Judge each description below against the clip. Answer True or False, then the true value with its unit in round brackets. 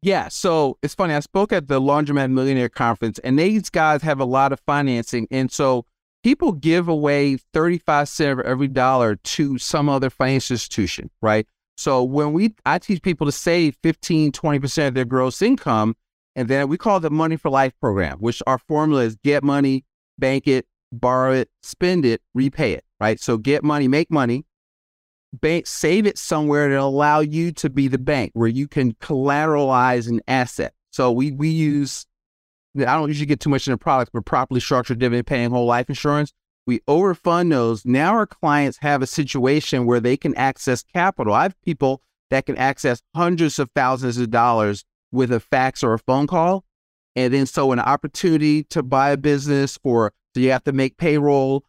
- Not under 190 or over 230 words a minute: True (195 wpm)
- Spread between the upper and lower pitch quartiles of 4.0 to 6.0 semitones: False (3.3 semitones)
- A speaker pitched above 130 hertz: True (140 Hz)